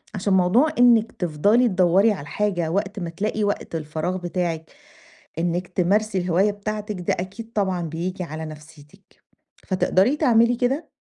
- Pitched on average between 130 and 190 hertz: Yes, medium, 185 Hz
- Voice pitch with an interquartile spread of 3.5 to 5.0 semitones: Yes, average, 3.8 semitones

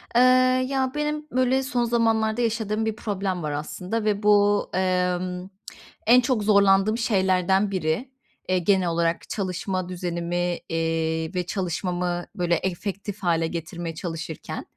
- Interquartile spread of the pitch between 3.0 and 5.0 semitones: Yes, average, 4.0 semitones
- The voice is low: No, high, 190 Hz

